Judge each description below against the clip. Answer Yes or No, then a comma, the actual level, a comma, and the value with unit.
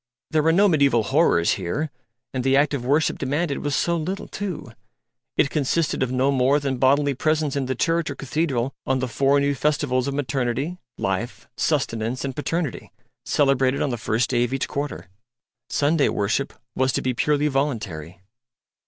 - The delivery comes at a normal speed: Yes, average, 175 wpm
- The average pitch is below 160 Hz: Yes, medium, 140 Hz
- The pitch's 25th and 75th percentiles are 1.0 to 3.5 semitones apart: Yes, average, 2.8 semitones